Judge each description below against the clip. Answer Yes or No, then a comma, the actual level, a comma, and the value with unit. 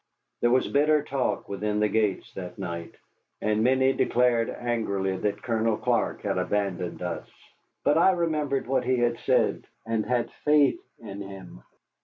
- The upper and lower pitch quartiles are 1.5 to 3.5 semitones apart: No, average, 4.8 semitones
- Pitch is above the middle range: No, low, 115 Hz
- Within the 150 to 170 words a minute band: Yes, average, 155 wpm